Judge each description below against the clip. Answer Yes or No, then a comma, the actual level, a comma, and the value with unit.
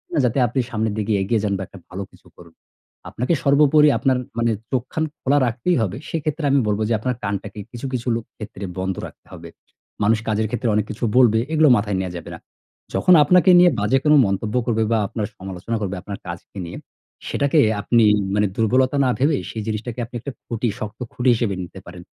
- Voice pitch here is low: Yes, low, 115 Hz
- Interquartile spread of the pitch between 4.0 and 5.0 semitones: Yes, average, 4.3 semitones